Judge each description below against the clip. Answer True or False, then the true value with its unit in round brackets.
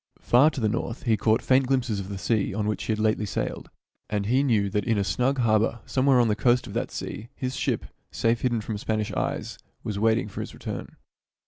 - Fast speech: True (230 wpm)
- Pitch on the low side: True (110 Hz)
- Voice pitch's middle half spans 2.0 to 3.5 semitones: True (2.9 semitones)